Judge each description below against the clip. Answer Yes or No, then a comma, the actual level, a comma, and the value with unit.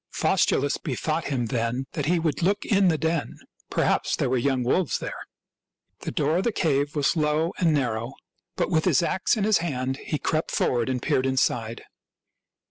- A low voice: No, medium, 145 Hz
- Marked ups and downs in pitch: No, average, 4.4 semitones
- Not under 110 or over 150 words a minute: No, average, 190 wpm